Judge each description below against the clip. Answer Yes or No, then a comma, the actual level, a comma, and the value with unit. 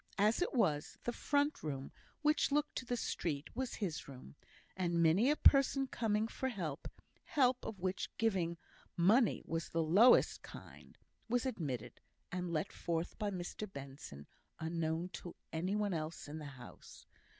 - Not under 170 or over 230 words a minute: No, average, 160 wpm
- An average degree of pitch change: No, wide, 6.7 semitones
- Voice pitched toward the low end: No, medium, 180 Hz